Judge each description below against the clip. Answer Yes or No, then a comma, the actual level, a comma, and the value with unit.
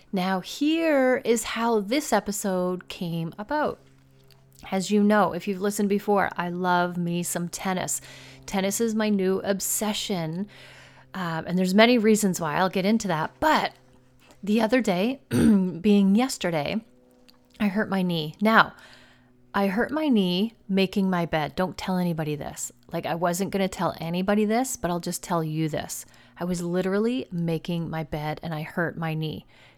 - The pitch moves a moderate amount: Yes, average, 4.1 semitones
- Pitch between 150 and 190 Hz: Yes, medium, 185 Hz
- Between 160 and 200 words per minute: Yes, average, 165 wpm